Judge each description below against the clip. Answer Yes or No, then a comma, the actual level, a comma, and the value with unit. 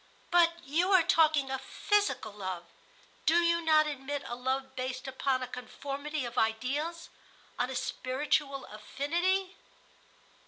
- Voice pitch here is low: No, very high, 280 Hz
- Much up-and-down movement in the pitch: No, average, 4.4 semitones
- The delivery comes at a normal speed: No, slow, 130 wpm